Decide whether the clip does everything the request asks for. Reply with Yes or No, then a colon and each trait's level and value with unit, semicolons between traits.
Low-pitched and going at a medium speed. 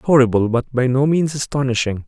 Yes: low, 130 Hz; average, 175 wpm